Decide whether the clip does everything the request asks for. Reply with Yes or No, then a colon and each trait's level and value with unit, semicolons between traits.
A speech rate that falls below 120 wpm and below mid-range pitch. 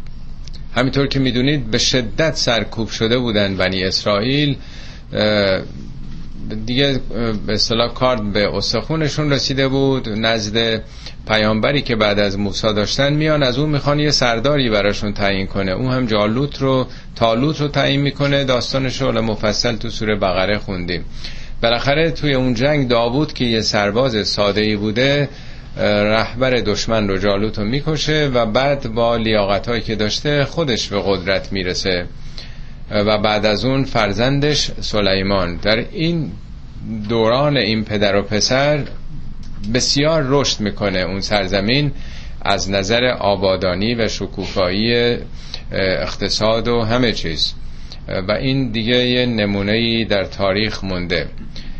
No: average, 125 wpm; low, 115 Hz